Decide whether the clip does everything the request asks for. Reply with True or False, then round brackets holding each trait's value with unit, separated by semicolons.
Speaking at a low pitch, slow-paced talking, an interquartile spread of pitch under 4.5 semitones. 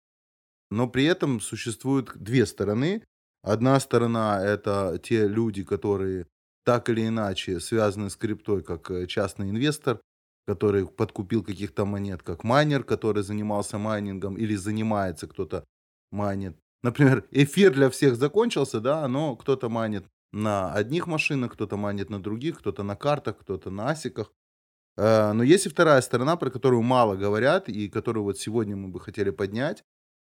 False (105 Hz; 145 wpm; 3.7 semitones)